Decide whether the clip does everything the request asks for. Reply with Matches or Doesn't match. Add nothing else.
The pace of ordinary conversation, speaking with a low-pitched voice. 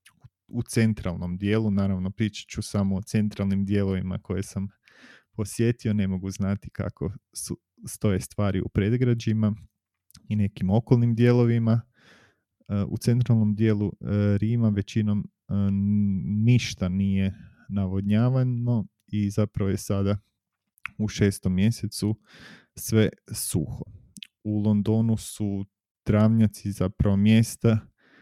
Doesn't match